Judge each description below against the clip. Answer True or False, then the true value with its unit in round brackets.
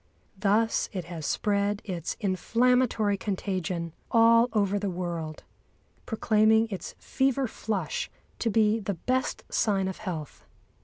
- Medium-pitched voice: False (205 Hz)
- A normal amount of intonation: True (3.5 semitones)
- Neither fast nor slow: False (120 wpm)